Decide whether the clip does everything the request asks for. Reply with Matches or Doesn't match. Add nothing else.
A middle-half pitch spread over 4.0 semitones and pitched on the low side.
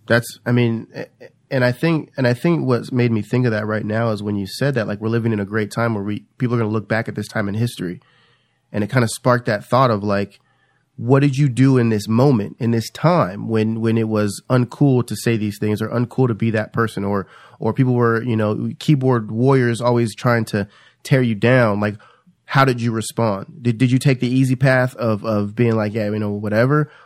Doesn't match